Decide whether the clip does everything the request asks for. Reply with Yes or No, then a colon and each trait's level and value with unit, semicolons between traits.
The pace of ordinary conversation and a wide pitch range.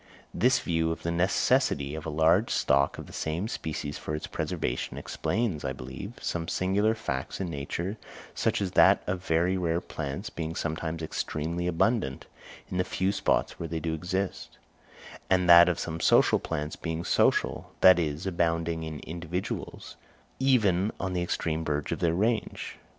No: average, 165 wpm; average, 2.8 semitones